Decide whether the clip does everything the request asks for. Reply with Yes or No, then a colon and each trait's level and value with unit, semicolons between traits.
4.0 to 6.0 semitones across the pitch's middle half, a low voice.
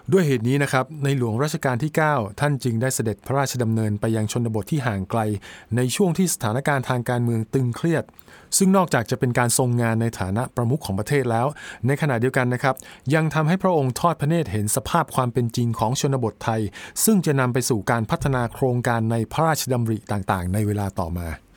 Yes: average, 4.3 semitones; low, 125 Hz